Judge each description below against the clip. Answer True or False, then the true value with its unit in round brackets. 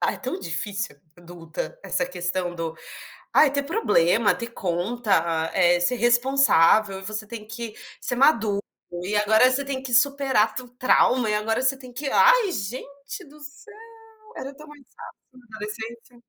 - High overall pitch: True (235 Hz)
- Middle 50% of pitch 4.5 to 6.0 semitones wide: True (5.4 semitones)